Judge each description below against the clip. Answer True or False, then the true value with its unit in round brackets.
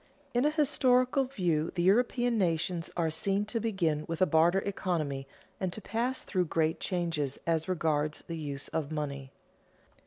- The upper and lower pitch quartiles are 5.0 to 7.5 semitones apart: True (5.4 semitones)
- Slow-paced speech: False (160 wpm)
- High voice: False (175 Hz)